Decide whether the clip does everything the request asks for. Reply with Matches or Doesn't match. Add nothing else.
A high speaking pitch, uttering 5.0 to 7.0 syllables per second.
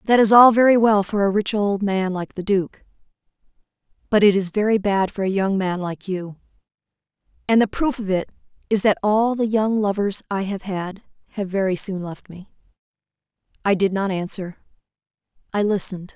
Matches